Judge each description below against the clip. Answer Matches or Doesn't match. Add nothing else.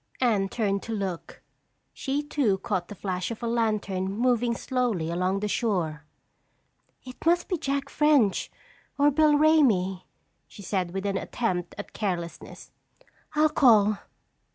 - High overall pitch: Matches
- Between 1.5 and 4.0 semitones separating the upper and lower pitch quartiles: Doesn't match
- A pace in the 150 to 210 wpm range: Doesn't match